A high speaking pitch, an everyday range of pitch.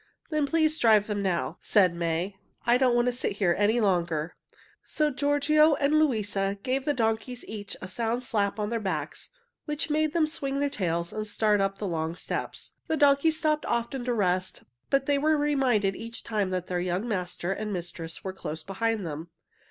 No: high, 220 Hz; wide, 6.8 semitones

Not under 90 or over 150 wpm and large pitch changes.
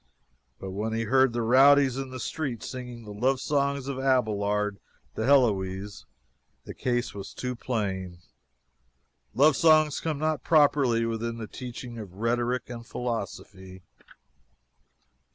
No: slow, 135 wpm; average, 4.0 semitones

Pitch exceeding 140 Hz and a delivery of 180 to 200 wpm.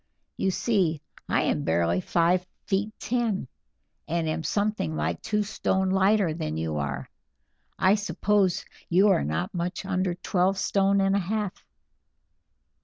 No: medium, 185 Hz; average, 140 wpm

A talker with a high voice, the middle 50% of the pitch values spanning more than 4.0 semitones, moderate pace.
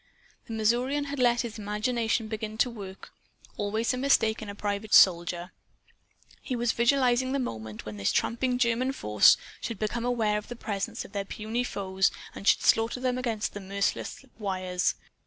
No: high, 220 Hz; average, 3.4 semitones; average, 175 wpm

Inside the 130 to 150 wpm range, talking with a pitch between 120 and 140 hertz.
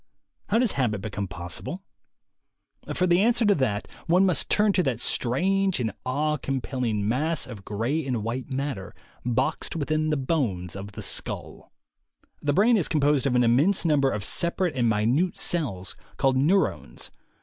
No: average, 160 wpm; low, 135 Hz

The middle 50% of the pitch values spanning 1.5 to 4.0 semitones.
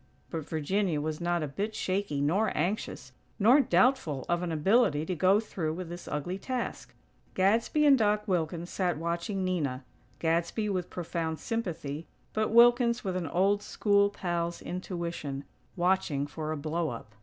No: average, 4.4 semitones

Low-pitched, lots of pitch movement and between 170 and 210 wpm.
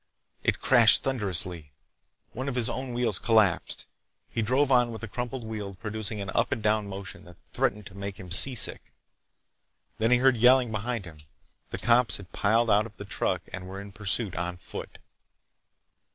No: low, 110 Hz; average, 3.6 semitones; average, 180 wpm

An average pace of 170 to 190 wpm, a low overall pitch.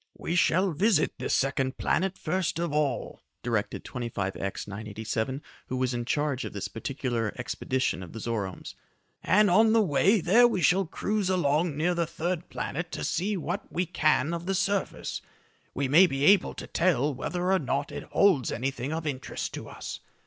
No: average, 180 wpm; medium, 155 Hz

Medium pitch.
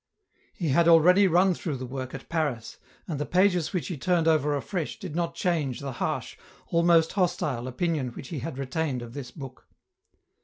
Yes: medium, 160 Hz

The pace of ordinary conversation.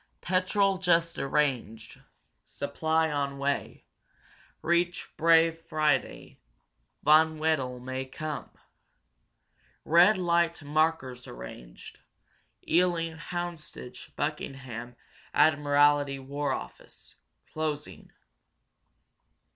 No: slow, 75 wpm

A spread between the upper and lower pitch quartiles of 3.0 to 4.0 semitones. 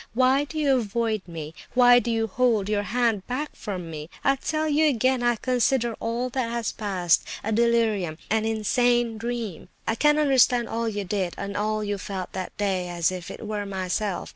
Yes: average, 3.7 semitones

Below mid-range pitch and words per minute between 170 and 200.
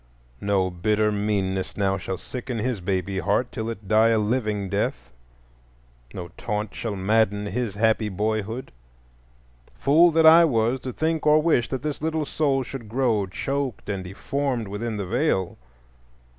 No: low, 110 Hz; average, 155 wpm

